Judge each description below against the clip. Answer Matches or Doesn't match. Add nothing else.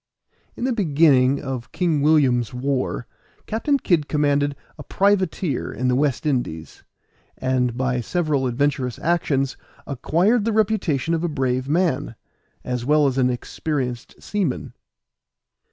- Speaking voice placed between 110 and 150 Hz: Matches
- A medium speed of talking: Doesn't match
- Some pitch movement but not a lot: Matches